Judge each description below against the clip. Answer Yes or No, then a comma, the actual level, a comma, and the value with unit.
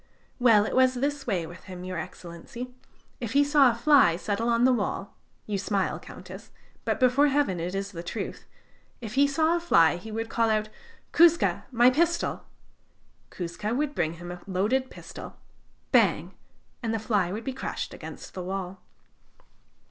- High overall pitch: Yes, high, 225 Hz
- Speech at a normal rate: Yes, average, 170 wpm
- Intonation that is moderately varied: No, wide, 5.8 semitones